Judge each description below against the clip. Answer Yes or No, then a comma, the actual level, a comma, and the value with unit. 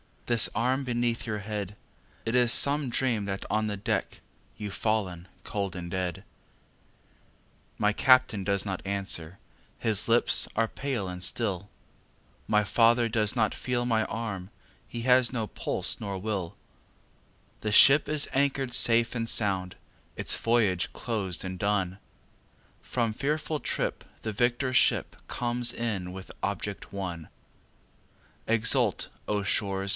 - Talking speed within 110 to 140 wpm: Yes, slow, 135 wpm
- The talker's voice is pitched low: Yes, low, 110 Hz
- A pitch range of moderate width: Yes, average, 3.5 semitones